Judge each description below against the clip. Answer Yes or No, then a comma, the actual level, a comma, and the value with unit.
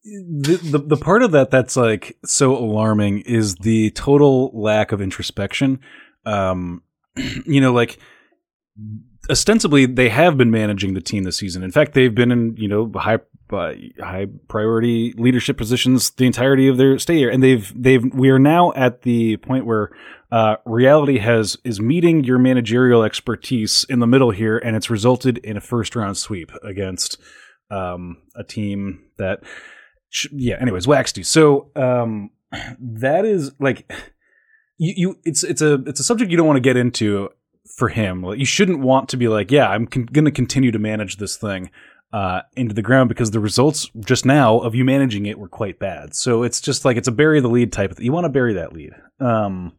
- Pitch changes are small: No, average, 3.9 semitones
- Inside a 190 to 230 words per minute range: Yes, average, 195 wpm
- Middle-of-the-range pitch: No, low, 120 Hz